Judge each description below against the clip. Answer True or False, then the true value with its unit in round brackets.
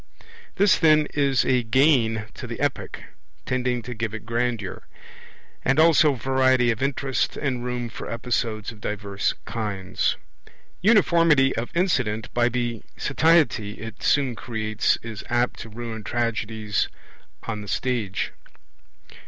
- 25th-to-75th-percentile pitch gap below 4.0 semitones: True (3.3 semitones)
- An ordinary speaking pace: False (130 wpm)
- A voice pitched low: True (120 Hz)